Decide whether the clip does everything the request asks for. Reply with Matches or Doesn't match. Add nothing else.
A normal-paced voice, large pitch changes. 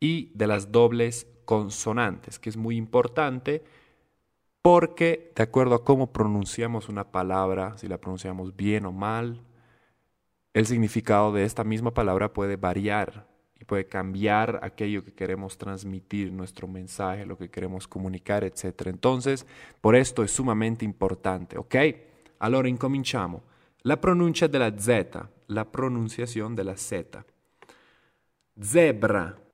Doesn't match